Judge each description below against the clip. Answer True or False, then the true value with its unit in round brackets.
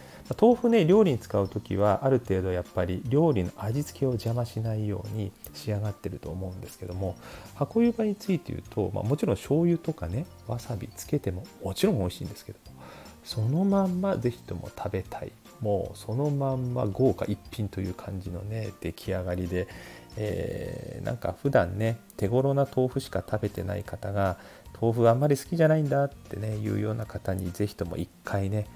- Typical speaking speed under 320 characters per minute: False (375 characters per minute)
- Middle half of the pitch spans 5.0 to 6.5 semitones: True (5.8 semitones)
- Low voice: True (105 Hz)